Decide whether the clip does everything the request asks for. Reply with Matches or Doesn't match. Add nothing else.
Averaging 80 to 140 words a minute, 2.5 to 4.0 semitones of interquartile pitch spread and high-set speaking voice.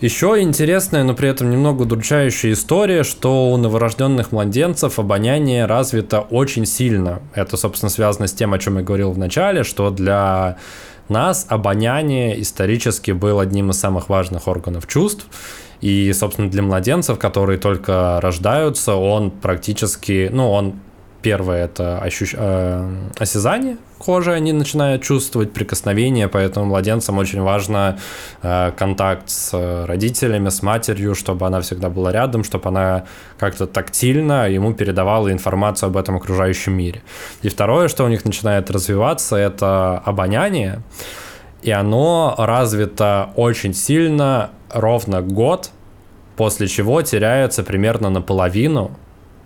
Doesn't match